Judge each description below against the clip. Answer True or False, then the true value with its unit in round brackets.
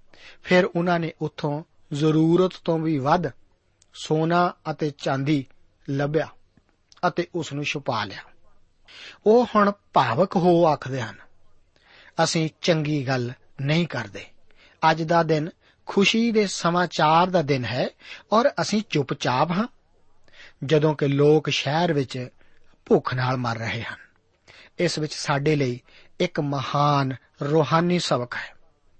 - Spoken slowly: False (125 wpm)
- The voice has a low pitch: False (155 Hz)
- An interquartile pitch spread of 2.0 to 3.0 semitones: False (3.8 semitones)